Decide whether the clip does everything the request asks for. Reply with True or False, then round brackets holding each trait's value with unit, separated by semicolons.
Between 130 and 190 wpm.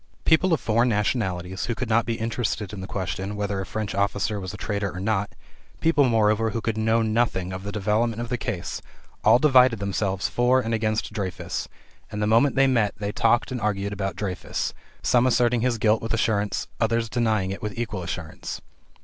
False (200 wpm)